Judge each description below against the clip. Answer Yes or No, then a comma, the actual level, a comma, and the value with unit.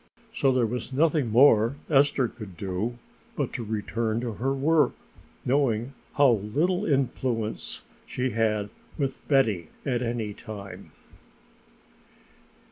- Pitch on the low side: Yes, low, 120 Hz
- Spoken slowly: Yes, slow, 125 wpm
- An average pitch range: Yes, average, 3.9 semitones